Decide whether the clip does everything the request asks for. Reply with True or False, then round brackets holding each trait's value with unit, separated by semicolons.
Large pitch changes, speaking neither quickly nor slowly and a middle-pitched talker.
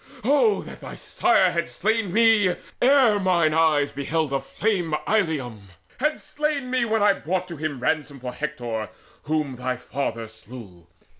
True (8.4 semitones; 150 wpm; 160 Hz)